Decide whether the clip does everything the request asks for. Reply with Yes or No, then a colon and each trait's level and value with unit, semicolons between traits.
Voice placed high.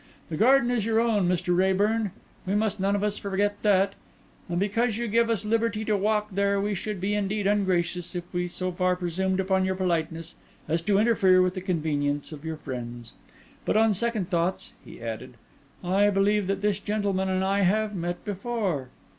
Yes: high, 195 Hz